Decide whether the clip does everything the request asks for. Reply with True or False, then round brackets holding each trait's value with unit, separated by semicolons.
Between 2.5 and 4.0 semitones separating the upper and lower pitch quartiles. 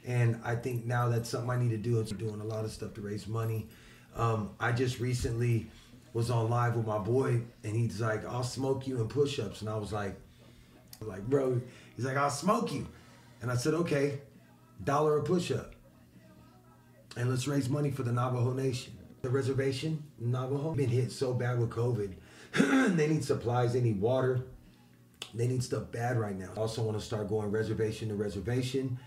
True (3.3 semitones)